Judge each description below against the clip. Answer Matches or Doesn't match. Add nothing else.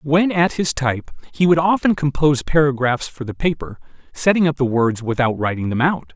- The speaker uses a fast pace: Doesn't match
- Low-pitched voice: Doesn't match